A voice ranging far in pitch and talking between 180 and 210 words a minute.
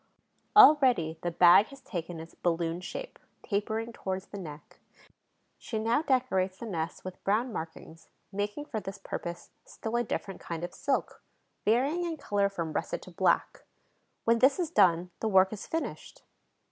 No: wide, 5.8 semitones; average, 160 wpm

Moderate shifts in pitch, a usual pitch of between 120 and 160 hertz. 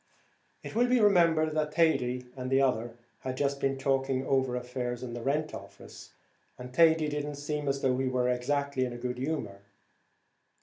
Yes: average, 3.1 semitones; low, 135 Hz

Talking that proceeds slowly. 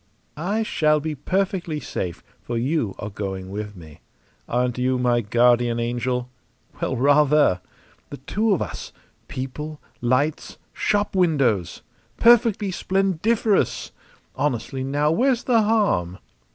Yes: slow, 120 wpm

